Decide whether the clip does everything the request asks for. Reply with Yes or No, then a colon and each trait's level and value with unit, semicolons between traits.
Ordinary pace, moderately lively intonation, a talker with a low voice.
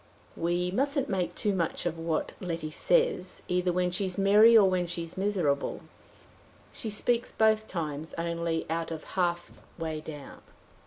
No: average, 150 wpm; average, 3.5 semitones; medium, 180 Hz